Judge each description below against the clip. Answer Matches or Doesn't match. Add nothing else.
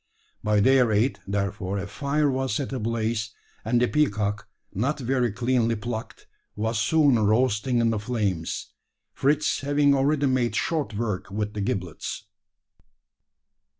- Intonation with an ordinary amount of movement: Matches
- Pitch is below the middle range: Matches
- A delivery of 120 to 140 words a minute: Matches